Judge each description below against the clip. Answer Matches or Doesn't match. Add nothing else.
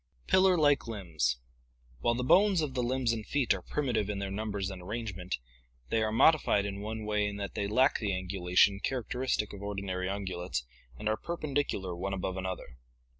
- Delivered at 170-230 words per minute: Matches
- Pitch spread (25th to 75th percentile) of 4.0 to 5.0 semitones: Matches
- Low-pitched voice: Matches